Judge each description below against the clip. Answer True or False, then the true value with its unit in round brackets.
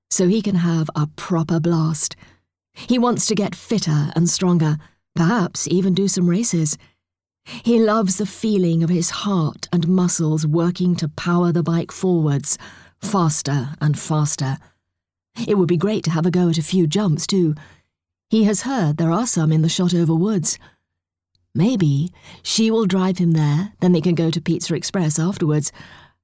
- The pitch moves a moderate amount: True (3.5 semitones)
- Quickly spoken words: False (170 wpm)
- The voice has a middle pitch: True (170 Hz)